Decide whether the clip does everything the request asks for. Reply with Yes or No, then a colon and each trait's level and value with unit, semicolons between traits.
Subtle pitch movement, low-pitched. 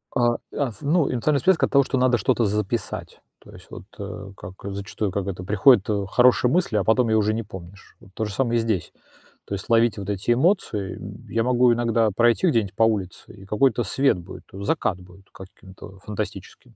No: average, 3.9 semitones; low, 110 Hz